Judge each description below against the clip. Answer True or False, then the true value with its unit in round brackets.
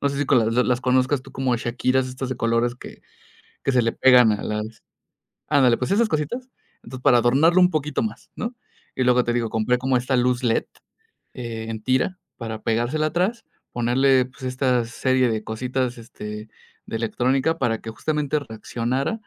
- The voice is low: True (125 Hz)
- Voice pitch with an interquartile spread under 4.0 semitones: True (2.5 semitones)